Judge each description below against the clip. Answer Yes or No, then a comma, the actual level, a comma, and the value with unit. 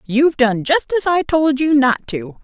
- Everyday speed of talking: No, fast, 220 wpm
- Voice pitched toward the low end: No, very high, 265 Hz